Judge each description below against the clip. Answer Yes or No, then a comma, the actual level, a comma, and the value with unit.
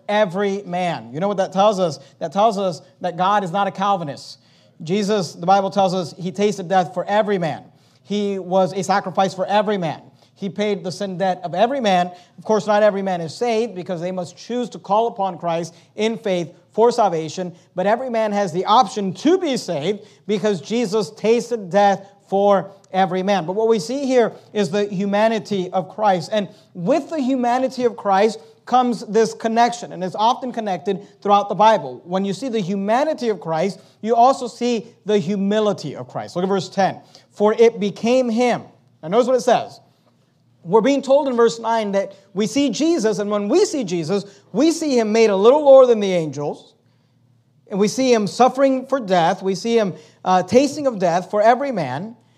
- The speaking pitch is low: No, high, 200 Hz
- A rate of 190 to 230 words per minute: Yes, average, 200 wpm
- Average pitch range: Yes, average, 3.6 semitones